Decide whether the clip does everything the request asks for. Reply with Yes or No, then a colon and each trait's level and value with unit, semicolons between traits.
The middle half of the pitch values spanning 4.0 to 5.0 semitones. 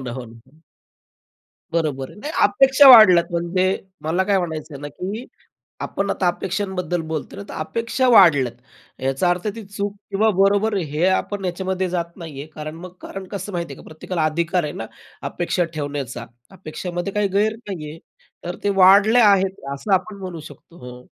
Yes: average, 4.3 semitones